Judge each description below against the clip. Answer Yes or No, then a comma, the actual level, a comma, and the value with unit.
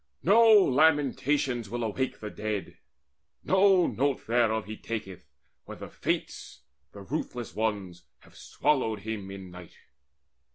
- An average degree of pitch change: No, wide, 5.8 semitones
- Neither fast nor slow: No, slow, 125 wpm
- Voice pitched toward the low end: Yes, low, 115 Hz